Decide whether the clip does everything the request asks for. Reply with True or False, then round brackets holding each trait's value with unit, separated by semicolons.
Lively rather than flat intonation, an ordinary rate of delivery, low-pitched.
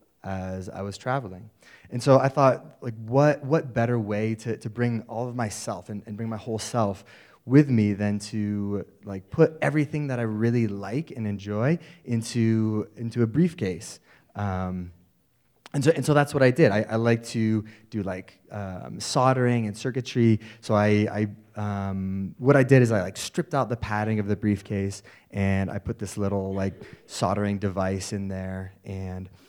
False (3.3 semitones; 180 wpm; 110 Hz)